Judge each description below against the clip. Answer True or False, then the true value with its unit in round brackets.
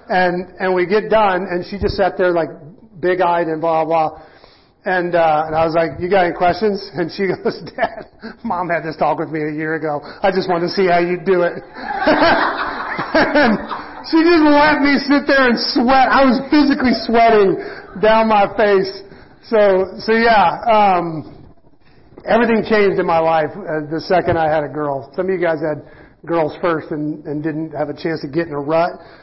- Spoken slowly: False (200 wpm)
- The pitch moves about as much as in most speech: True (5.0 semitones)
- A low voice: False (180 Hz)